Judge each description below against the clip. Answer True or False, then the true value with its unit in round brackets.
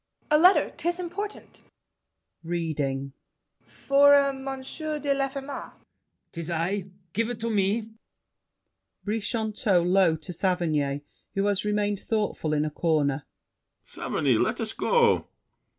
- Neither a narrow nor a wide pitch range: False (8.6 semitones)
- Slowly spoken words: True (120 wpm)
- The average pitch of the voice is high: True (205 Hz)